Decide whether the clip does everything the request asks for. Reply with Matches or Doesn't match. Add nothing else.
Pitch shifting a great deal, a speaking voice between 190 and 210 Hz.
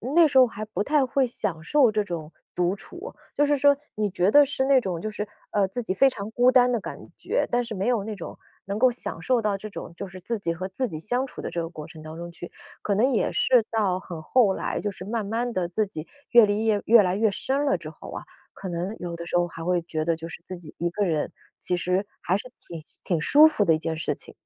Matches